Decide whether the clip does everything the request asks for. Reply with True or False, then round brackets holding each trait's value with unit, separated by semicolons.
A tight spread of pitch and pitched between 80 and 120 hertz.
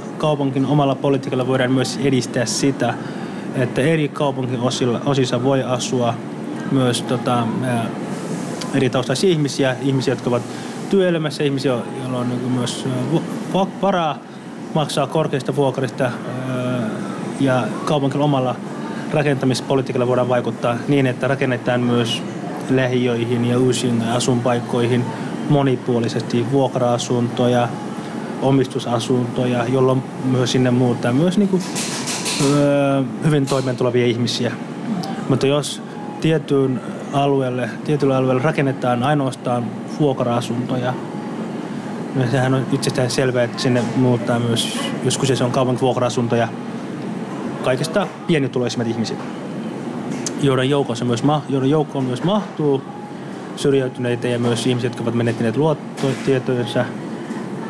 False (2.2 semitones; 130 Hz)